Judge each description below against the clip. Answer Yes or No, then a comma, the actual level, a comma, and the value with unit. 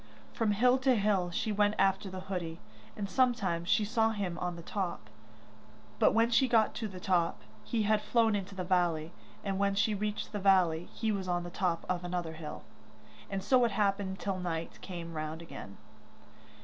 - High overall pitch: Yes, high, 195 Hz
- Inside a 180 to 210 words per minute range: Yes, average, 190 wpm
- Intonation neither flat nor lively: Yes, average, 3.4 semitones